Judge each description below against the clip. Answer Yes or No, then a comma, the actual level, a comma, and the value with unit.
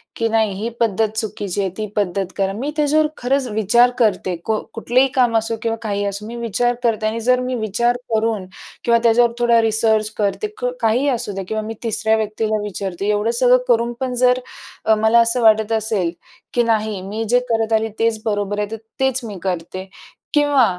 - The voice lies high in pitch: Yes, high, 220 Hz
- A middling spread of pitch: No, narrow, 2.3 semitones